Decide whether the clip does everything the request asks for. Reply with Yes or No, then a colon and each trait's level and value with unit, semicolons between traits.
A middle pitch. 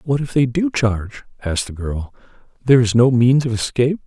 No: low, 125 Hz